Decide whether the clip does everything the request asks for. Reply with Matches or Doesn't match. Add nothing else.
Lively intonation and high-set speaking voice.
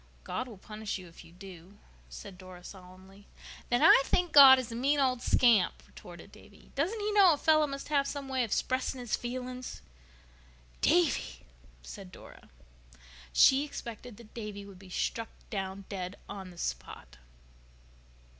Matches